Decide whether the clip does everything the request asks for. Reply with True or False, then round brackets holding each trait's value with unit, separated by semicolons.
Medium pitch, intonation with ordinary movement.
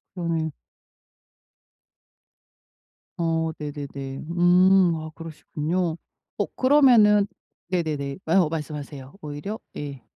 True (165 Hz; 3.6 semitones)